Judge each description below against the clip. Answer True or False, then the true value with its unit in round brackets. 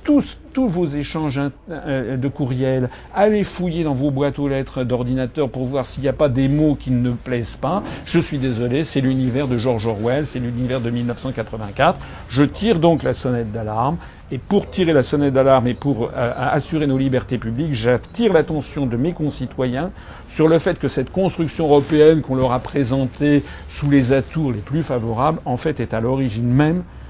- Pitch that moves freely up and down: False (3.3 semitones)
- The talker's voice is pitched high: False (135 Hz)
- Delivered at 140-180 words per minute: False (190 wpm)